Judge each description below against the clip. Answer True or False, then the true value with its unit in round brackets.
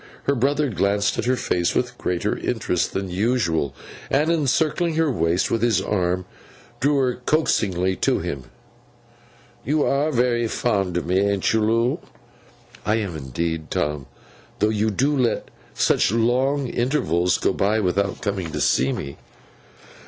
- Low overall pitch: True (110 Hz)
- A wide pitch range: True (6.0 semitones)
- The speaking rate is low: False (150 wpm)